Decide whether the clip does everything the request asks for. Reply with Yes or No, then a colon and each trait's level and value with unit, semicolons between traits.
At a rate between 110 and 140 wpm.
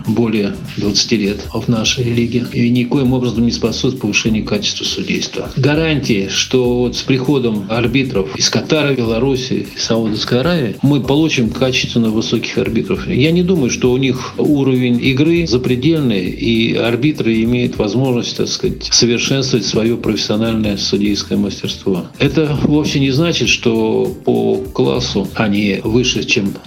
Yes: average, 135 wpm